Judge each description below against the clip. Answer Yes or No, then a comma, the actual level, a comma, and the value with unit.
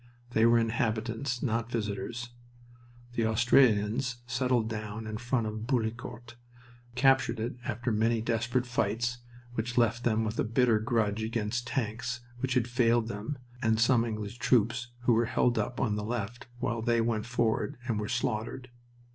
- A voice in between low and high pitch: No, low, 115 Hz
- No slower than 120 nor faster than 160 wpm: Yes, average, 155 wpm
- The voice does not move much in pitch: Yes, narrow, 1.8 semitones